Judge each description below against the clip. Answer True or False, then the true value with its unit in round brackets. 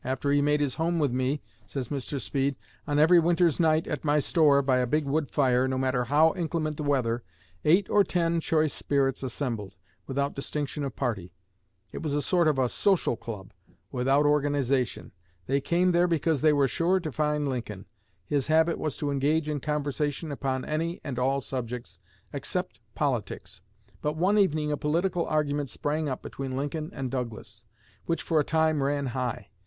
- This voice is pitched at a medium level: True (145 Hz)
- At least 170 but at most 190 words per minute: True (180 wpm)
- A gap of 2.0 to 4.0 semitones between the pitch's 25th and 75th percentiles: True (3.1 semitones)